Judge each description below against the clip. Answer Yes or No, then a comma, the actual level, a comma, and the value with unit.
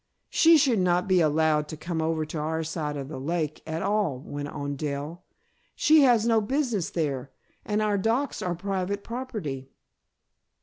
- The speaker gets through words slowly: No, average, 170 wpm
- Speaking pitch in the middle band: Yes, medium, 170 Hz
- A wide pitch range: Yes, wide, 5.7 semitones